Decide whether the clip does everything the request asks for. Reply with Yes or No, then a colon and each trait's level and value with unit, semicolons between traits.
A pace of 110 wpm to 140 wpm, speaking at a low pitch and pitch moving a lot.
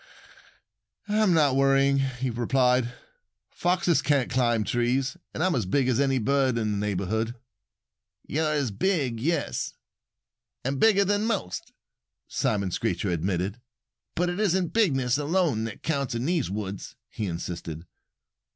Yes: slow, 135 wpm; low, 130 Hz; wide, 6.2 semitones